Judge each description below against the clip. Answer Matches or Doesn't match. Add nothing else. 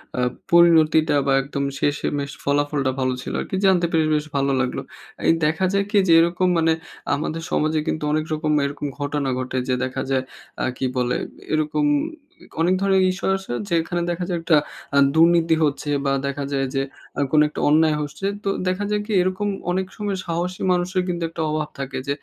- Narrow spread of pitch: Doesn't match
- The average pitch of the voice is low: Doesn't match